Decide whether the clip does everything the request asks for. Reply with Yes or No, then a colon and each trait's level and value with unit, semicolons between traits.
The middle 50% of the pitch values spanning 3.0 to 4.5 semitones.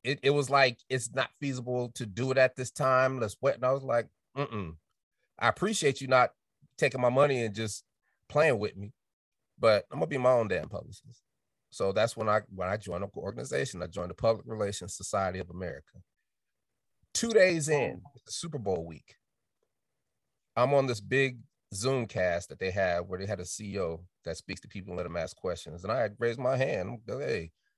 No: average, 5.0 semitones